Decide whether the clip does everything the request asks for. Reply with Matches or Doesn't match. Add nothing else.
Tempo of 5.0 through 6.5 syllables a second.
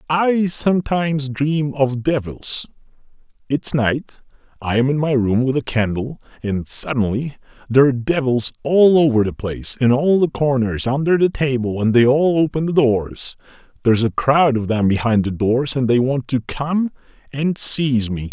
Doesn't match